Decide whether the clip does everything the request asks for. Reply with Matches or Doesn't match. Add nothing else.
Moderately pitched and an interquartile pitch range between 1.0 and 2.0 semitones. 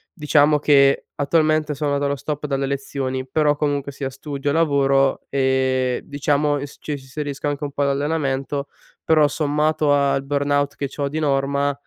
Matches